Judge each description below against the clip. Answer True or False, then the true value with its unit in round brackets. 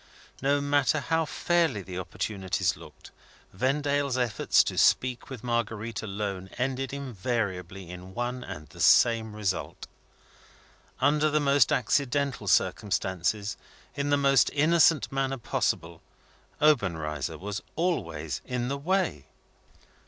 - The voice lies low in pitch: True (125 Hz)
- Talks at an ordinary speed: False (115 wpm)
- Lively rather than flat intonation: True (6.5 semitones)